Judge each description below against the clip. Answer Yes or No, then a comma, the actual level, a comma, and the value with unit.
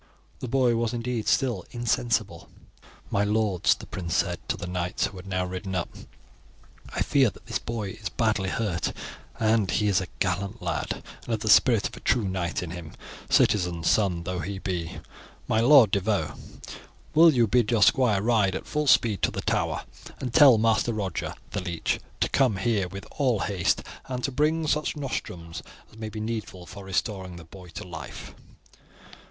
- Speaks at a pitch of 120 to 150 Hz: No, low, 105 Hz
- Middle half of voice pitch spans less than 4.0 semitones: No, average, 4.4 semitones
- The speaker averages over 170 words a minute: Yes, average, 185 wpm